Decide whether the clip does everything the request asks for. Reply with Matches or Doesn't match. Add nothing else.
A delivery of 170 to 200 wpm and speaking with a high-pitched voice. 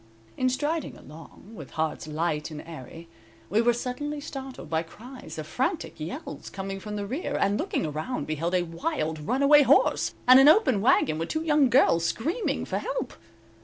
Matches